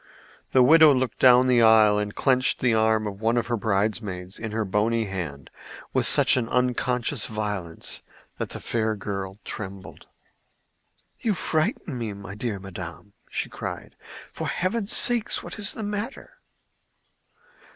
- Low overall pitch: Yes, low, 110 Hz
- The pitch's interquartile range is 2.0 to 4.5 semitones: Yes, average, 4.0 semitones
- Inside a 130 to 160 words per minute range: Yes, average, 145 wpm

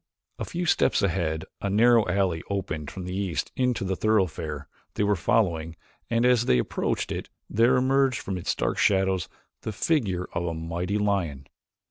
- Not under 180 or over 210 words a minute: No, average, 170 wpm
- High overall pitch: No, very low, 95 Hz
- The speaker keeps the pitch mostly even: No, average, 4.9 semitones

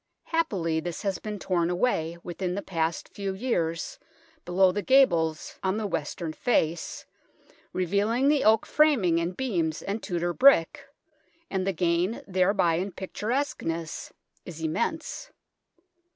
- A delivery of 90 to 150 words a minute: Yes, slow, 135 wpm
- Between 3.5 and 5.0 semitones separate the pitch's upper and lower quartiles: Yes, average, 4.3 semitones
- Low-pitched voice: No, medium, 185 Hz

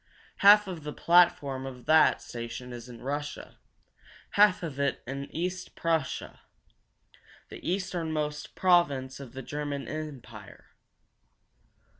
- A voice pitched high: No, medium, 150 Hz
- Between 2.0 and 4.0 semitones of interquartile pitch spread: No, average, 4.6 semitones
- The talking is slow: Yes, slow, 115 wpm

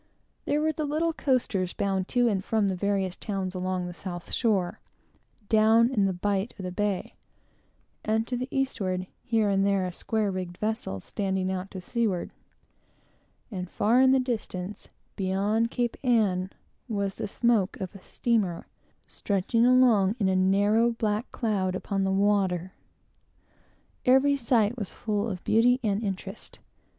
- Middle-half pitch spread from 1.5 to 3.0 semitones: No, average, 3.6 semitones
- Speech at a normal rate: Yes, average, 155 wpm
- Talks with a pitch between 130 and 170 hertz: No, high, 205 Hz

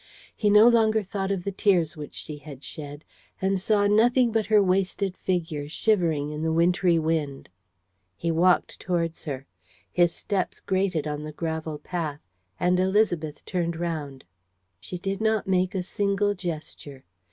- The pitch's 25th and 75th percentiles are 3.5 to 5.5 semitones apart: Yes, average, 4.1 semitones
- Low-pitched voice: No, medium, 175 Hz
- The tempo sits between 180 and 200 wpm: No, average, 155 wpm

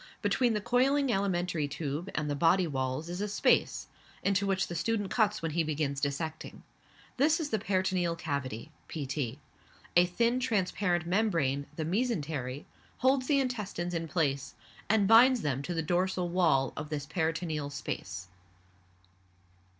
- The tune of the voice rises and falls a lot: Yes, wide, 5.7 semitones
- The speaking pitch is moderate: Yes, medium, 175 Hz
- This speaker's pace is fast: No, average, 150 wpm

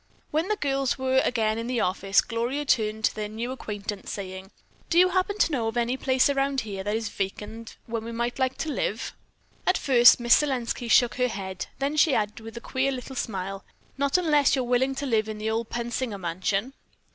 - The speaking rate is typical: No, fast, 210 wpm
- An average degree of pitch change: Yes, average, 3.9 semitones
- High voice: Yes, high, 235 Hz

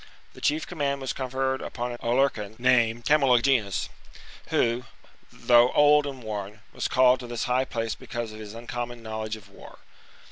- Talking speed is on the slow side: No, average, 170 wpm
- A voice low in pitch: Yes, low, 120 Hz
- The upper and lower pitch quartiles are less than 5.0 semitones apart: Yes, average, 2.9 semitones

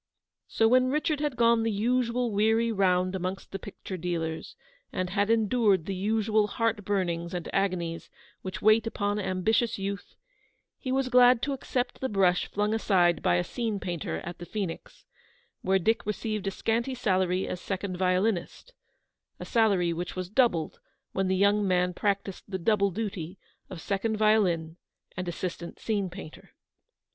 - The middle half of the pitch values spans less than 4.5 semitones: Yes, average, 3.6 semitones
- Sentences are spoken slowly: No, average, 160 wpm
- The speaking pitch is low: No, high, 200 Hz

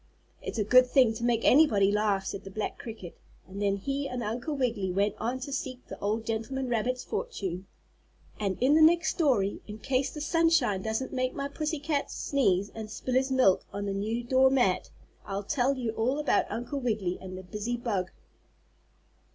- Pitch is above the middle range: Yes, high, 235 Hz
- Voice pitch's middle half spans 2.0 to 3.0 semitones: No, average, 4.7 semitones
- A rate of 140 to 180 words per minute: No, average, 190 wpm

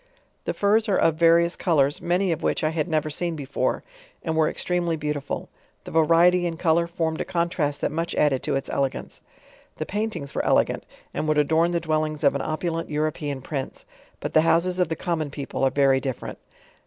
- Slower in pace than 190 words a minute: No, fast, 205 wpm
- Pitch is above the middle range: No, medium, 160 Hz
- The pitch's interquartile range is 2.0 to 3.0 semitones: Yes, narrow, 2.4 semitones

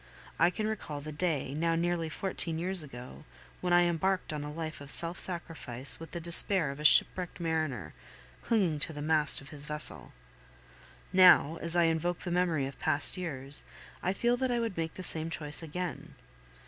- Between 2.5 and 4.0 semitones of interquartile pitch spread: Yes, average, 3.2 semitones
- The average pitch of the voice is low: No, medium, 165 Hz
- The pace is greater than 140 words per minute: Yes, average, 185 wpm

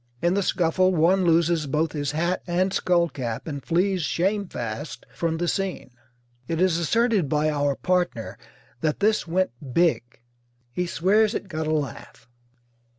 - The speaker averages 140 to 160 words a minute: Yes, average, 155 wpm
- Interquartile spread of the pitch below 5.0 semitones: Yes, average, 3.6 semitones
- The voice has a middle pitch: Yes, medium, 170 Hz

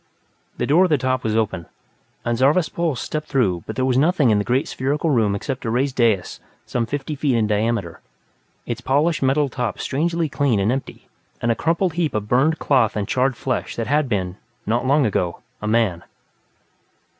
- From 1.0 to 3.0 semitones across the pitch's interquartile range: No, average, 4.6 semitones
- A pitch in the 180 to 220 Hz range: No, low, 130 Hz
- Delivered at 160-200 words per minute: Yes, average, 195 wpm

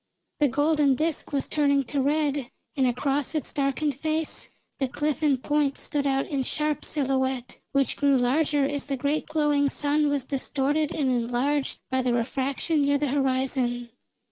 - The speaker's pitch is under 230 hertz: No, very high, 280 Hz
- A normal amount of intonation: No, narrow, 1.9 semitones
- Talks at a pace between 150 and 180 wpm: Yes, average, 165 wpm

